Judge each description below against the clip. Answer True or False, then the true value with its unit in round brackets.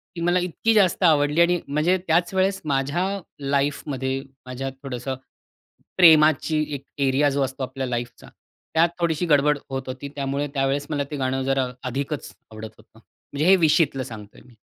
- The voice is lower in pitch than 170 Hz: True (140 Hz)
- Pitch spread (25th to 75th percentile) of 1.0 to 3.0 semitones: False (3.4 semitones)